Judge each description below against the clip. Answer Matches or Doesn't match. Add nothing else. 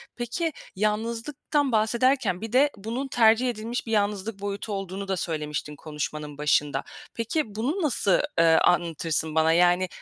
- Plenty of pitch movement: Matches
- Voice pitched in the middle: Doesn't match